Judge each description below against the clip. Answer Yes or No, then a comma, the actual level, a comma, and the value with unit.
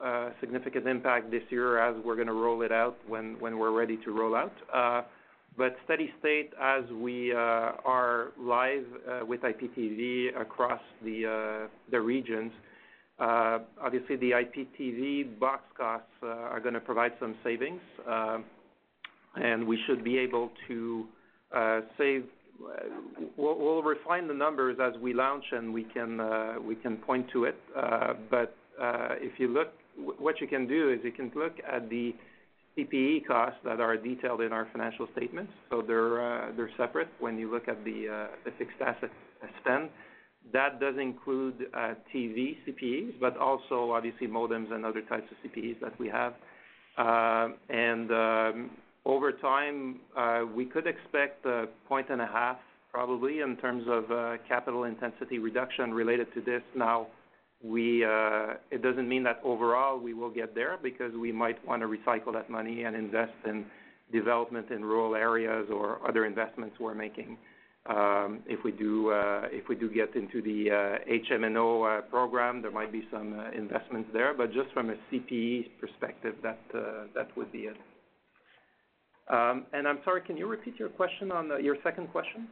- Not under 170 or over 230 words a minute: Yes, average, 175 wpm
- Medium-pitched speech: No, low, 120 Hz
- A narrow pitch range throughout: Yes, narrow, 2.1 semitones